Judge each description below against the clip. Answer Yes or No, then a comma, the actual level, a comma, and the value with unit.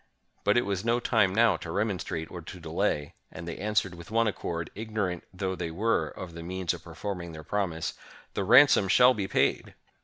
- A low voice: Yes, very low, 95 Hz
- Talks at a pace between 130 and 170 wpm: No, fast, 205 wpm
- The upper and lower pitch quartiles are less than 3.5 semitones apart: No, average, 4.1 semitones